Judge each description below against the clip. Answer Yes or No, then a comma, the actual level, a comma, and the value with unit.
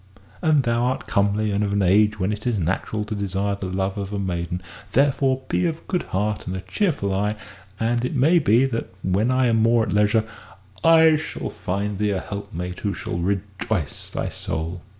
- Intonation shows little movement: No, average, 3.8 semitones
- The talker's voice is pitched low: Yes, low, 105 Hz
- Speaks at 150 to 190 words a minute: No, average, 200 wpm